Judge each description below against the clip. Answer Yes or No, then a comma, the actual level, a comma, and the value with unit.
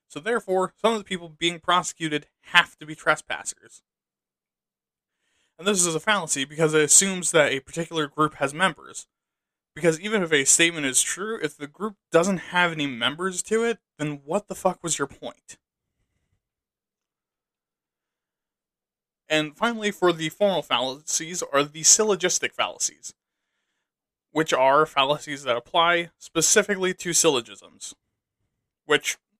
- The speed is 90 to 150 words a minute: Yes, average, 140 wpm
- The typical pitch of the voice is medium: Yes, medium, 170 Hz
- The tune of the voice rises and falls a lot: No, average, 3.9 semitones